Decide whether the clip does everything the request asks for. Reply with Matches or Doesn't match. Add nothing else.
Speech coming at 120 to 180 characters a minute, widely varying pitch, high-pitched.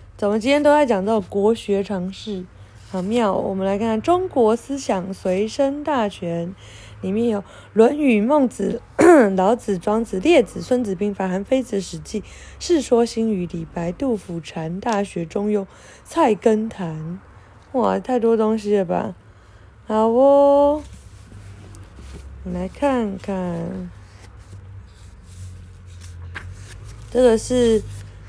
Matches